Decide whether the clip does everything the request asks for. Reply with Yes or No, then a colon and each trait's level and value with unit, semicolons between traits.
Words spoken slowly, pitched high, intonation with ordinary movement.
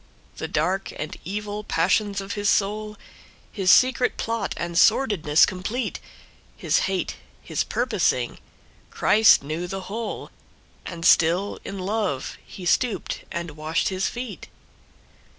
Yes: slow, 115 wpm; high, 195 Hz; average, 3.8 semitones